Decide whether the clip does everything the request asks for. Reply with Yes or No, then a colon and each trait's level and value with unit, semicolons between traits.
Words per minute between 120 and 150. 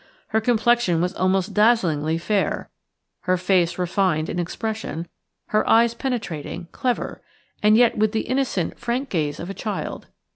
Yes: average, 145 wpm